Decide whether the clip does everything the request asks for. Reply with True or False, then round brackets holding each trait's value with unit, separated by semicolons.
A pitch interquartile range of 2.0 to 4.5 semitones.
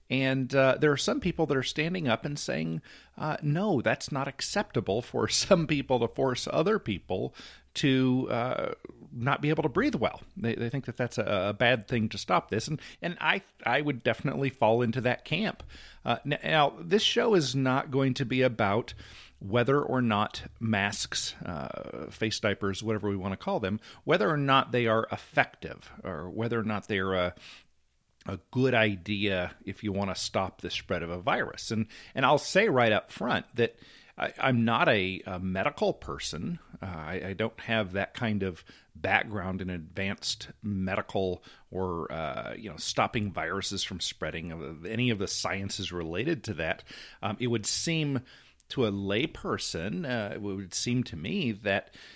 False (5.2 semitones)